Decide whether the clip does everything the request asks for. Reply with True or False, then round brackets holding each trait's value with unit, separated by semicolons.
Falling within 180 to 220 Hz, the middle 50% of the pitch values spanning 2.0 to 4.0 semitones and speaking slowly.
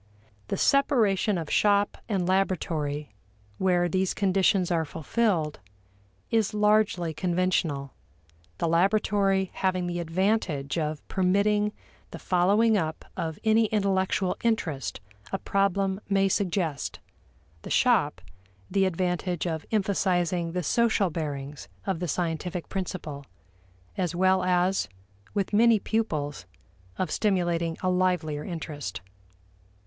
True (185 Hz; 3.3 semitones; 115 wpm)